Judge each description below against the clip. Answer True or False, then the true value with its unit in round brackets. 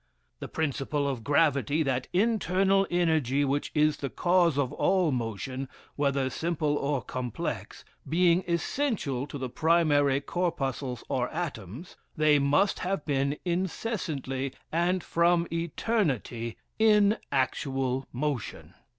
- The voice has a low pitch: False (145 Hz)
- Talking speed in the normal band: False (115 wpm)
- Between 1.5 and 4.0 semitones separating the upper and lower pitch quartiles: False (4.5 semitones)